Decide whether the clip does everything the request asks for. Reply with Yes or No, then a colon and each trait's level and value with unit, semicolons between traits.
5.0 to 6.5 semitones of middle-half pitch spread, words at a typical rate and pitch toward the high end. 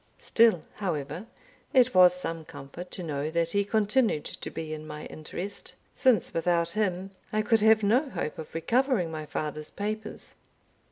No: average, 5.3 semitones; average, 160 wpm; medium, 180 Hz